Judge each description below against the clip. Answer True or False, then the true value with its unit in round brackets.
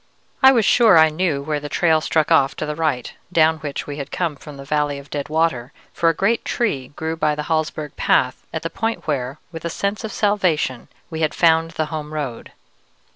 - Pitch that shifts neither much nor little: False (2.2 semitones)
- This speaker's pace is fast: True (220 wpm)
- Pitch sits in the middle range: True (155 Hz)